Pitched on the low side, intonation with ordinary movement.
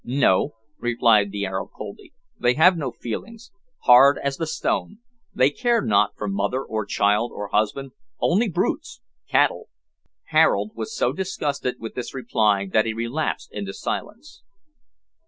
No: low, 120 Hz; wide, 6.3 semitones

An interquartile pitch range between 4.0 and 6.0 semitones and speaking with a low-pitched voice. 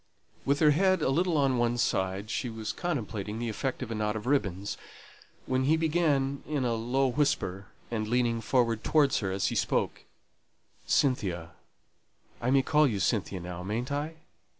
Yes: average, 5.0 semitones; low, 120 Hz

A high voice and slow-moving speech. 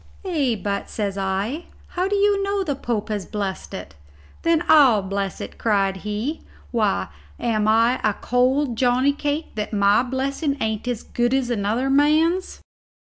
No: high, 245 Hz; average, 160 wpm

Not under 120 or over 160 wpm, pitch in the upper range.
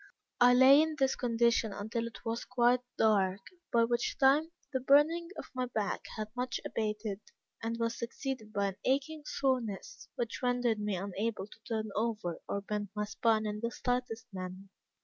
No: average, 170 wpm; high, 230 Hz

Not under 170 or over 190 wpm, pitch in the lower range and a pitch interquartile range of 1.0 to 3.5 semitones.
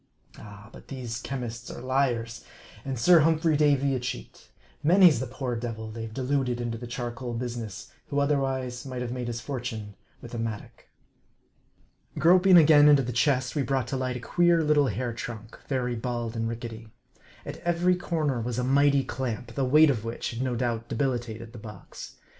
Yes: average, 180 wpm; low, 125 Hz; average, 3.2 semitones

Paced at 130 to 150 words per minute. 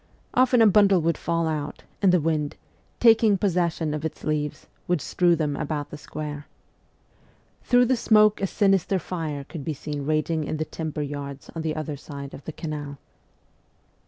No: average, 175 wpm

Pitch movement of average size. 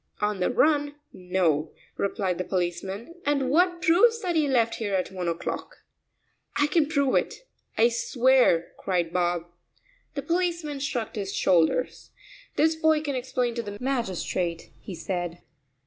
No: wide, 8.2 semitones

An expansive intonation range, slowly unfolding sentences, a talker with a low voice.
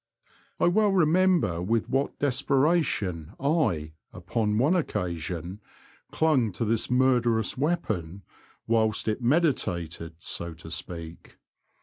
Yes: wide, 9.0 semitones; slow, 105 wpm; low, 115 Hz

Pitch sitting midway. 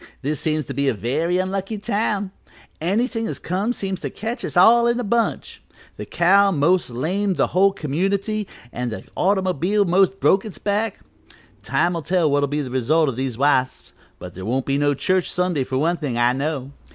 Yes: medium, 175 Hz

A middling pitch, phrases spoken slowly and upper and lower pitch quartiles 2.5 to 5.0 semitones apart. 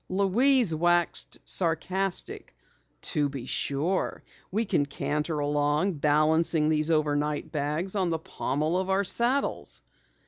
Yes: medium, 160 Hz; slow, 115 wpm; average, 4.2 semitones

